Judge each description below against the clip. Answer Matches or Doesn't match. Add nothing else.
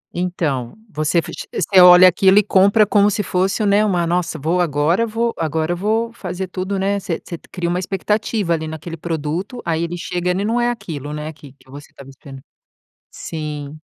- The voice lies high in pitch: Doesn't match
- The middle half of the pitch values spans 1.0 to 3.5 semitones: Doesn't match